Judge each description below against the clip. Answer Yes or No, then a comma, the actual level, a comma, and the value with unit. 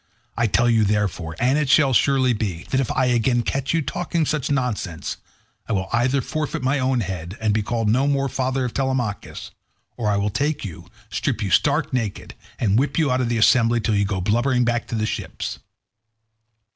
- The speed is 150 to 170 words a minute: No, average, 195 wpm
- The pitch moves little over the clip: No, average, 4.0 semitones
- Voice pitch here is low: Yes, low, 120 Hz